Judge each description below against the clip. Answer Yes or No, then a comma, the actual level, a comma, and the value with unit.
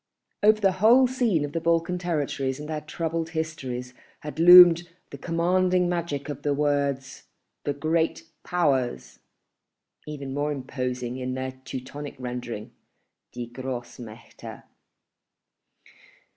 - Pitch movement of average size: Yes, average, 4.5 semitones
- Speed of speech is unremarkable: No, slow, 115 wpm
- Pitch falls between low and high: Yes, medium, 145 Hz